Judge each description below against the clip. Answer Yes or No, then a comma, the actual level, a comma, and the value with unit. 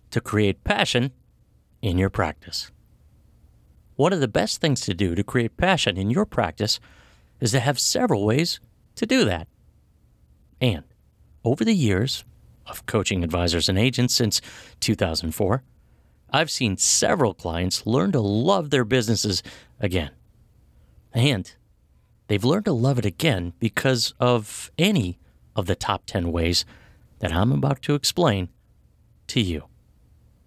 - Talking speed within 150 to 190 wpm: No, average, 140 wpm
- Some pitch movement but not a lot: No, wide, 6.1 semitones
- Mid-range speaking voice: No, low, 105 Hz